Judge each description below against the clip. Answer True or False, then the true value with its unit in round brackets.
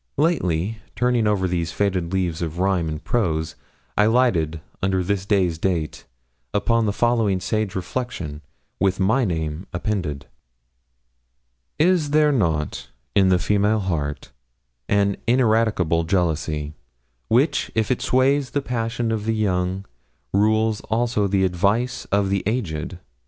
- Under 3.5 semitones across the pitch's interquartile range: False (4.5 semitones)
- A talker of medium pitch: False (100 Hz)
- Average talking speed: False (130 wpm)